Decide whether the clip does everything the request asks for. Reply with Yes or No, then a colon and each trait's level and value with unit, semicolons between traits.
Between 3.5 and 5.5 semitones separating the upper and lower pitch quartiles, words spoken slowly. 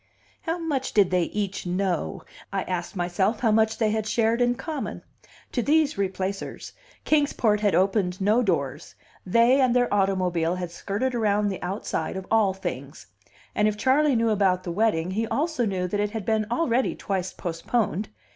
No: average, 4.0 semitones; average, 175 wpm